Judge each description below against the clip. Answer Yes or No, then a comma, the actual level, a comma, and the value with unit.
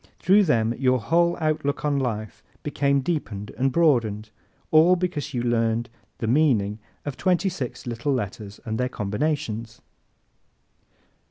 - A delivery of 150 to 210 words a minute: No, slow, 135 wpm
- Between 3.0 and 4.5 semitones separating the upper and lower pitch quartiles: No, wide, 5.5 semitones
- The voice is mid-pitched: No, low, 130 Hz